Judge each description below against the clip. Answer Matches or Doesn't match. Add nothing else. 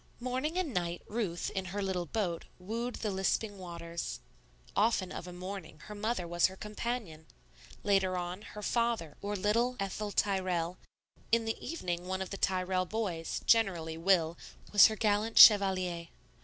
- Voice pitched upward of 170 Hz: Matches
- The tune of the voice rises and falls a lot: Doesn't match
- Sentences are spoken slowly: Doesn't match